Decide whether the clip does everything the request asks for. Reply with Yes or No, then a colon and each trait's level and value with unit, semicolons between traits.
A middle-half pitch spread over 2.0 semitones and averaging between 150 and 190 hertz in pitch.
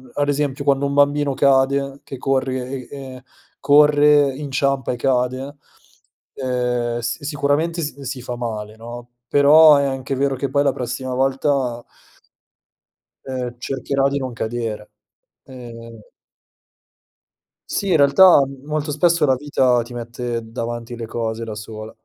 No: average, 2.8 semitones; low, 135 Hz